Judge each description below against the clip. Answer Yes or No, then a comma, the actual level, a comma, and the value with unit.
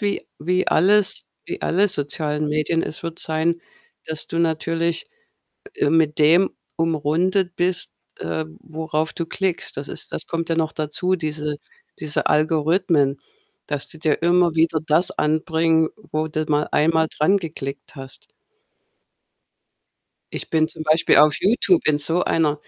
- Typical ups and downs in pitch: No, narrow, 1.9 semitones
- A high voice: No, medium, 160 Hz